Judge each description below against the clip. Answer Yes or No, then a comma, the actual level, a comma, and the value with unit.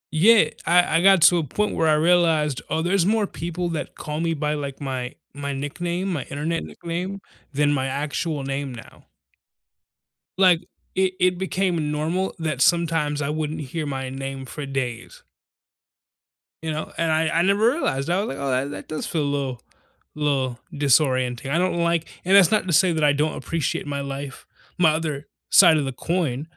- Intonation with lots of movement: No, average, 3.6 semitones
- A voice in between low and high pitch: Yes, medium, 155 Hz